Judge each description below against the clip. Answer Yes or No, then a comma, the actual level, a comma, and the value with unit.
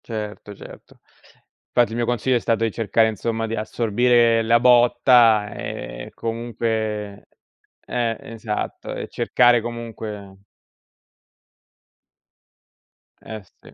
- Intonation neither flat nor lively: No, narrow, 1.7 semitones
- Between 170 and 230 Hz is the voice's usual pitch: No, low, 115 Hz